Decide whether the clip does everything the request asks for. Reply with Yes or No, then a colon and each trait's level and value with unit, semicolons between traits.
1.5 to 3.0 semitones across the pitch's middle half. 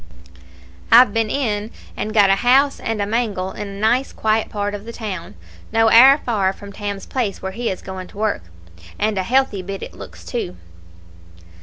Yes: average, 2.7 semitones